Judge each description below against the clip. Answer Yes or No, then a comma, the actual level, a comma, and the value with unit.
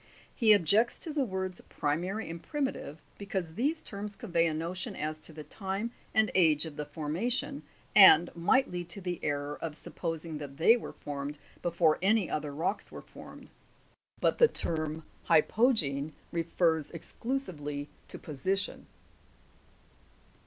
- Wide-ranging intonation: No, average, 4.8 semitones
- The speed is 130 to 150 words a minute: Yes, average, 145 wpm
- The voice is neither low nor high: Yes, medium, 170 Hz